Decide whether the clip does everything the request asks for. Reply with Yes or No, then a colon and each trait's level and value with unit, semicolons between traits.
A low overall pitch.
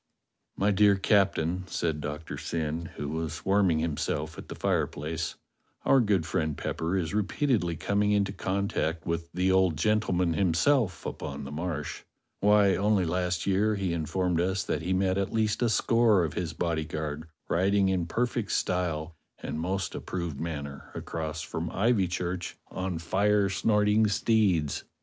Yes: very low, 90 Hz